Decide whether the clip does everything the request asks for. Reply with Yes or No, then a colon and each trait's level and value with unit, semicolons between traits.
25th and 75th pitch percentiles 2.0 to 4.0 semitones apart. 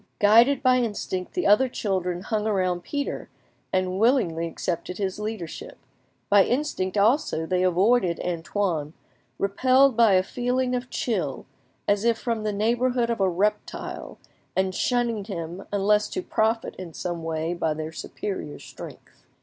No: average, 4.7 semitones